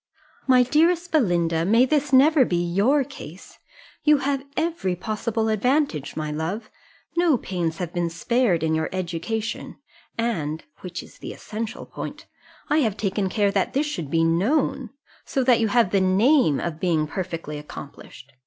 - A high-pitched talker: Yes, high, 200 Hz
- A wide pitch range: Yes, wide, 7.5 semitones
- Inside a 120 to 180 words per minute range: Yes, average, 160 wpm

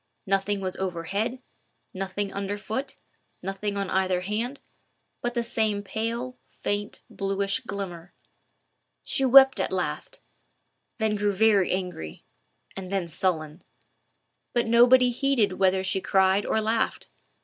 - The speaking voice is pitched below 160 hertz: No, high, 200 Hz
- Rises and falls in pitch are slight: No, average, 3.4 semitones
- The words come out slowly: Yes, slow, 125 wpm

